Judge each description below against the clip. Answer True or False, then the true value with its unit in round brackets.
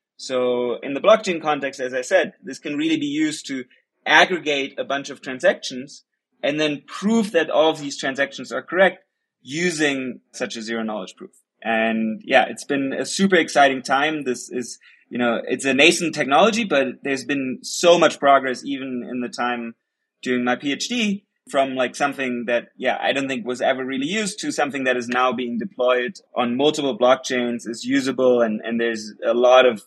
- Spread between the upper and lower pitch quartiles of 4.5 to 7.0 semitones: False (3.2 semitones)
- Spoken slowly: False (190 wpm)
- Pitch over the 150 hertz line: False (135 Hz)